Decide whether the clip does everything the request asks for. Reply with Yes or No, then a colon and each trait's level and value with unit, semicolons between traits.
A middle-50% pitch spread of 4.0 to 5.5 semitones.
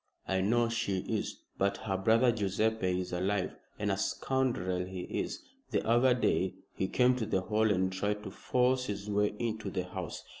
No: average, 3.5 semitones